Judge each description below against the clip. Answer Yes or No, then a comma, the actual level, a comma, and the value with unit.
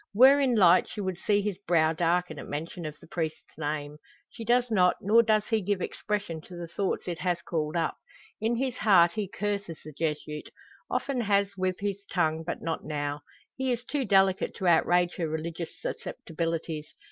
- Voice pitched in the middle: Yes, medium, 180 Hz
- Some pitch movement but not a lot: Yes, average, 4.2 semitones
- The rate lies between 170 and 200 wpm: Yes, average, 190 wpm